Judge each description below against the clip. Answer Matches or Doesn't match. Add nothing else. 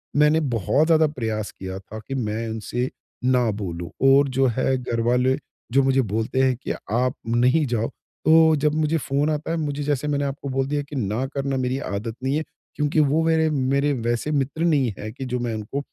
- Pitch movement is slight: Doesn't match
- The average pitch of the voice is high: Doesn't match